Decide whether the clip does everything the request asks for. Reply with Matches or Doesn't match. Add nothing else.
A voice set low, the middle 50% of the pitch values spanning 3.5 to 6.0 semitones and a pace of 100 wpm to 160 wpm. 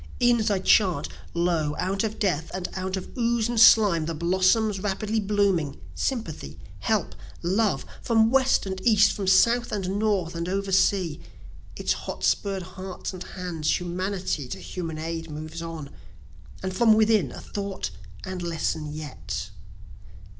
Doesn't match